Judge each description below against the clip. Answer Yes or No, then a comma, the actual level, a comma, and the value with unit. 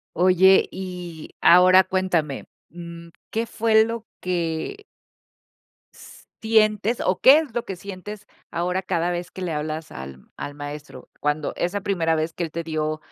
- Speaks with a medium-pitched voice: Yes, medium, 180 Hz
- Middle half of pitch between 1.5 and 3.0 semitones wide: No, average, 3.7 semitones